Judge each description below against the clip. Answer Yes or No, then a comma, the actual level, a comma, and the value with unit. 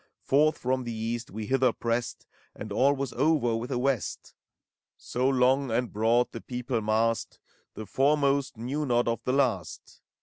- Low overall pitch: Yes, low, 125 Hz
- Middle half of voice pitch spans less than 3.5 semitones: Yes, average, 2.8 semitones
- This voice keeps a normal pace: Yes, average, 165 wpm